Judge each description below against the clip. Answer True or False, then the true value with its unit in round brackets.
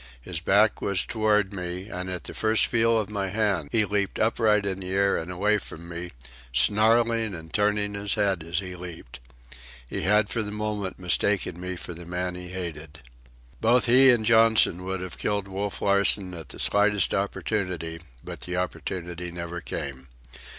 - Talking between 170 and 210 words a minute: True (180 wpm)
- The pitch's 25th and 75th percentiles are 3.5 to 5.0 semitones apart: False (3.1 semitones)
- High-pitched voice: False (95 Hz)